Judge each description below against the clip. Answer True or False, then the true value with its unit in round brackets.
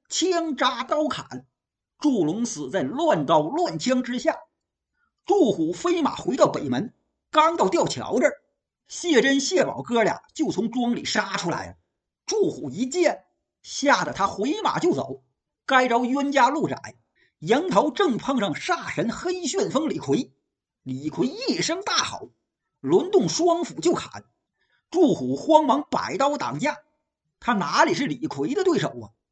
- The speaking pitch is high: True (305 Hz)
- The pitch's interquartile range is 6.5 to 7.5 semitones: False (5.6 semitones)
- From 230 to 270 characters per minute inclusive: False (205 characters per minute)